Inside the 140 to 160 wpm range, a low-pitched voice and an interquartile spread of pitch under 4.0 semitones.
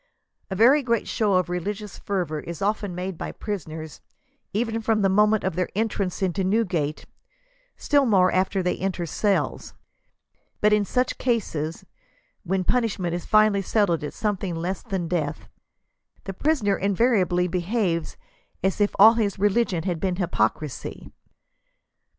No: average, 150 wpm; high, 195 Hz; average, 3.2 semitones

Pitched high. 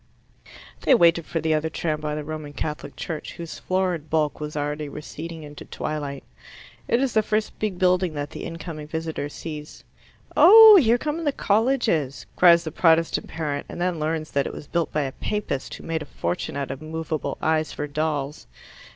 No: medium, 160 Hz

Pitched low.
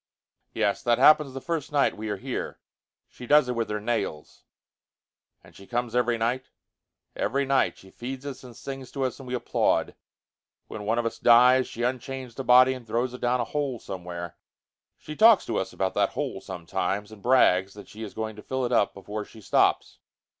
Yes: low, 120 Hz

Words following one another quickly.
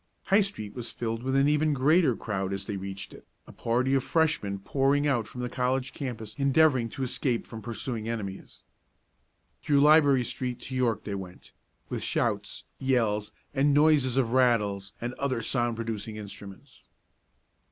No: average, 165 wpm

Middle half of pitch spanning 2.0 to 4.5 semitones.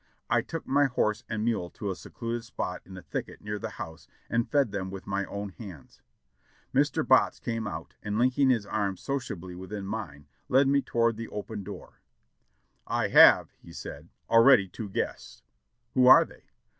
Yes: average, 3.4 semitones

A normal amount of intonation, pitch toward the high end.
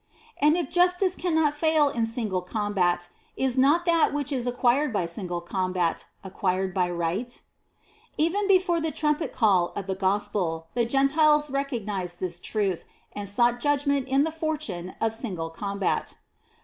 No: wide, 8.0 semitones; high, 240 Hz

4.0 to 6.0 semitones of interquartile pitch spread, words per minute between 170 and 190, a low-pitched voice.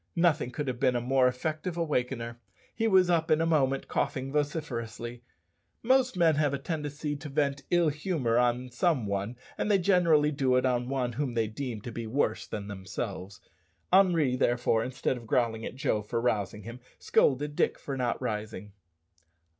Yes: average, 4.6 semitones; average, 180 wpm; low, 130 Hz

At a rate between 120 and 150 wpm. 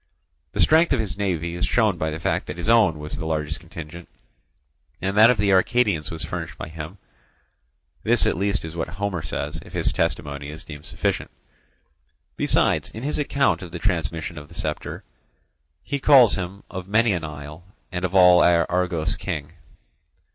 No: average, 180 wpm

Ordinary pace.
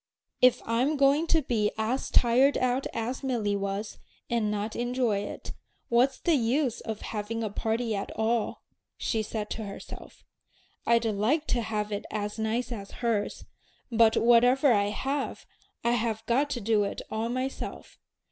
Yes: average, 160 wpm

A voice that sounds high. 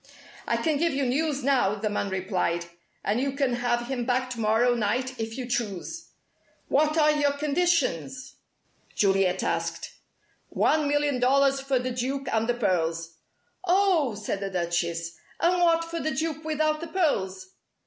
Yes: very high, 255 Hz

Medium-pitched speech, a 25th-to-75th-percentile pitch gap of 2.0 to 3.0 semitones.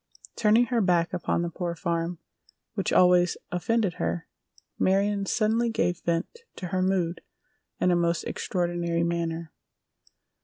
Yes: medium, 175 Hz; narrow, 2.6 semitones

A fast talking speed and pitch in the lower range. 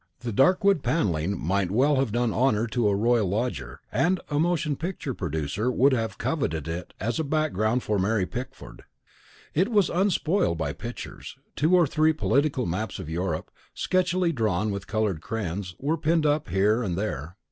No: average, 175 wpm; low, 120 Hz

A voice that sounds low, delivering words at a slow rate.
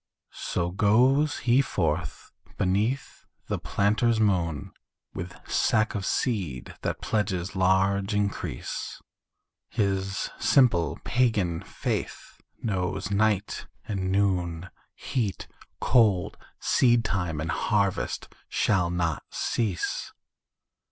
Yes: low, 100 Hz; slow, 90 wpm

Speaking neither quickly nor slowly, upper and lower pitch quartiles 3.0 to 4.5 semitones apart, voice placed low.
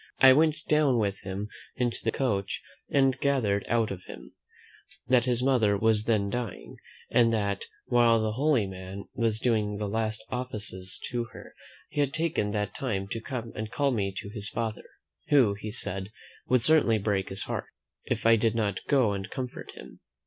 Yes: average, 180 wpm; average, 3.7 semitones; low, 110 Hz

